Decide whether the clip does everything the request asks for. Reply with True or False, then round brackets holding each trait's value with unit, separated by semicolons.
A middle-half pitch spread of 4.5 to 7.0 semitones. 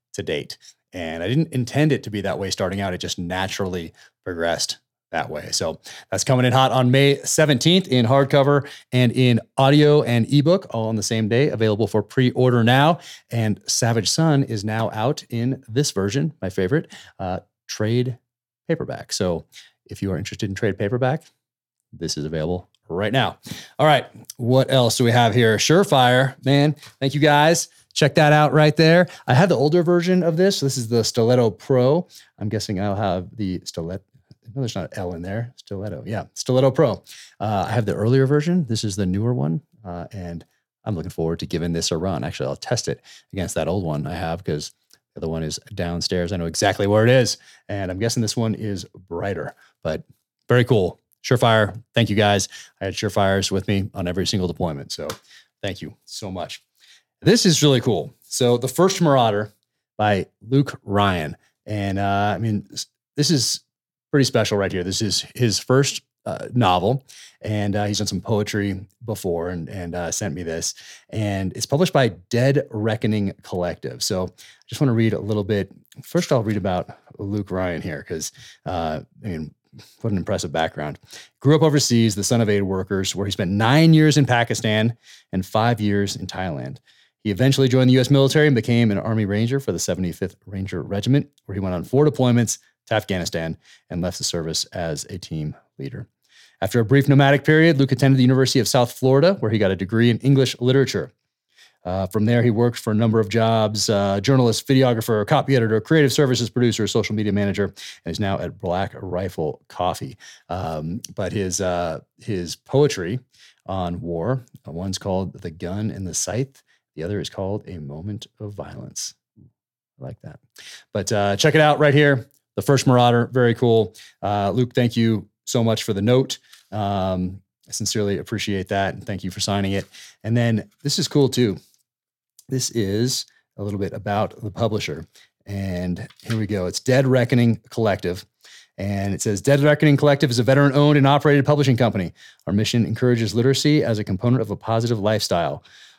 True (5.0 semitones)